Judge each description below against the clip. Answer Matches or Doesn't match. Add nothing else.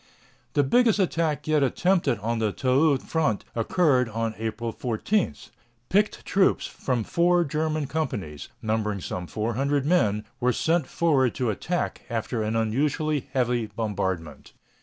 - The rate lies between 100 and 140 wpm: Matches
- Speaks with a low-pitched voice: Matches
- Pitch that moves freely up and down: Matches